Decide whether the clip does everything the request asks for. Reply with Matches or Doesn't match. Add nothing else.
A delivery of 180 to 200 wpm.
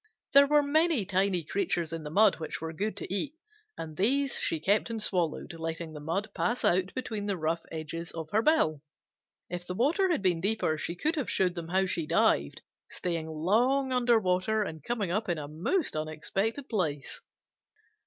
Matches